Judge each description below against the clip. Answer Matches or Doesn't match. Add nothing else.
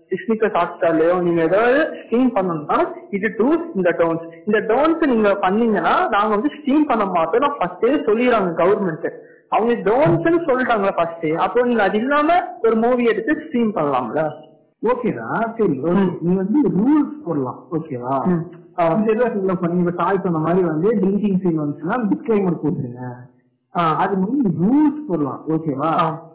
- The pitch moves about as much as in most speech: Doesn't match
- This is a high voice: Matches